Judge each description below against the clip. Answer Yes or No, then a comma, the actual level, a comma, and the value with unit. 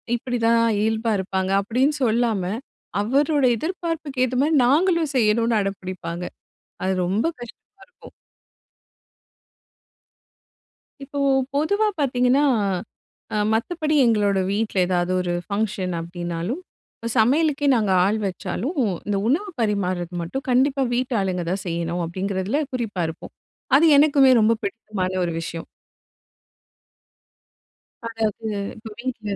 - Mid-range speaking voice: No, high, 225 Hz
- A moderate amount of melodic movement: No, wide, 6.1 semitones